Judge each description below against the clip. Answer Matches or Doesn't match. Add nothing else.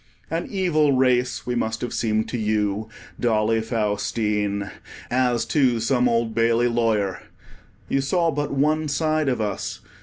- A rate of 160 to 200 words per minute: Doesn't match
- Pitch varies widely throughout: Doesn't match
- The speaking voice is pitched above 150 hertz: Doesn't match